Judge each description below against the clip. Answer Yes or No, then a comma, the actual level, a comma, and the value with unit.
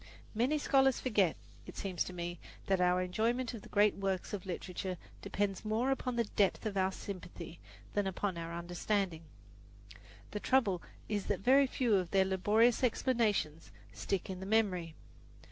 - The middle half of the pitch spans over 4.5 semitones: No, average, 3.7 semitones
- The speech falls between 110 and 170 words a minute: Yes, average, 160 wpm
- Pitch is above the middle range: Yes, high, 195 Hz